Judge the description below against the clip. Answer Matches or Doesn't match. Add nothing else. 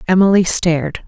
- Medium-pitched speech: Matches